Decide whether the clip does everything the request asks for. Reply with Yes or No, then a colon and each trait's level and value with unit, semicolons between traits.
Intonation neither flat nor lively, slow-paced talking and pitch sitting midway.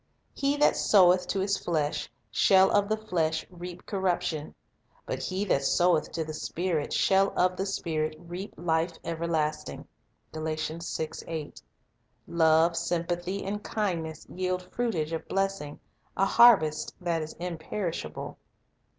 Yes: average, 3.2 semitones; slow, 130 wpm; medium, 175 Hz